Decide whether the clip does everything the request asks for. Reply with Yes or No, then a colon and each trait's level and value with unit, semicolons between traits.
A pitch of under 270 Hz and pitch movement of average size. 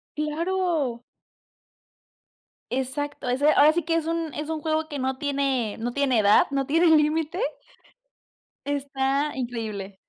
No: very high, 285 Hz; average, 3.3 semitones